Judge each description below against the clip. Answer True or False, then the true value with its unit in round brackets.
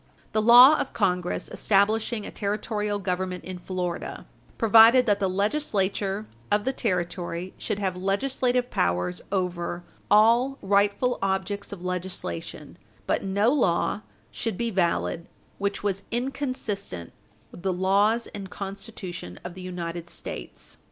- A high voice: True (195 Hz)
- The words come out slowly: True (130 wpm)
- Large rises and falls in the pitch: False (3.3 semitones)